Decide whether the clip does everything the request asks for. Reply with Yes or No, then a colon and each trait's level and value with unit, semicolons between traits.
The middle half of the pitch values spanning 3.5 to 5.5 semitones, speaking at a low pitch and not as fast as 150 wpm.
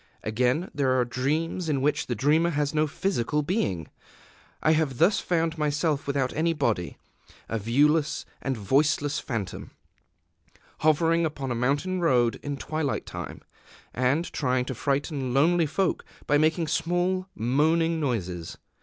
No: average, 4.2 semitones; medium, 145 Hz; average, 140 wpm